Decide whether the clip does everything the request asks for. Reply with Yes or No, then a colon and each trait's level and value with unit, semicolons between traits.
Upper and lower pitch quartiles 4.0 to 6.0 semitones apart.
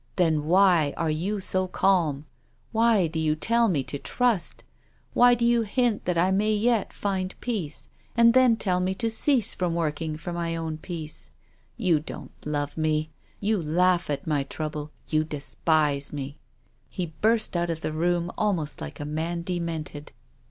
Yes: average, 4.7 semitones